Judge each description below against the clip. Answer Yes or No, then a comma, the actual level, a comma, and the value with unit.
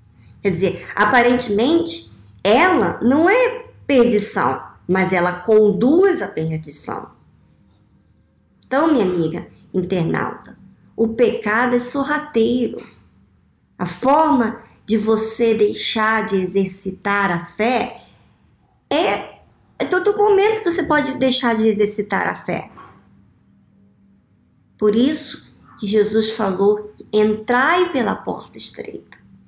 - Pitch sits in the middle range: No, high, 220 Hz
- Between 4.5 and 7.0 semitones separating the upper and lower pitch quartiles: Yes, average, 5.2 semitones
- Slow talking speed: Yes, slow, 105 wpm